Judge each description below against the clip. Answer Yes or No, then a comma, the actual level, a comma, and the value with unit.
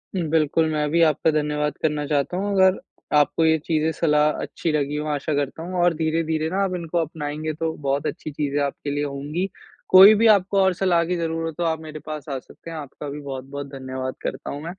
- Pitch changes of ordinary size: No, narrow, 2.2 semitones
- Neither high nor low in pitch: Yes, medium, 155 Hz